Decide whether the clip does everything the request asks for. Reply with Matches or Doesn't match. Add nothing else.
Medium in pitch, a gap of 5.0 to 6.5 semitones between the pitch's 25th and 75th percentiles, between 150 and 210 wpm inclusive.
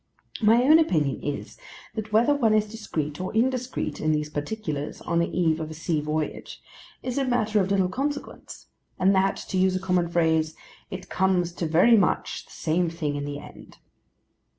Matches